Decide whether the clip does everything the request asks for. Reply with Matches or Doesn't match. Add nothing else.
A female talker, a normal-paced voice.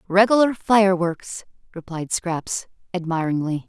Doesn't match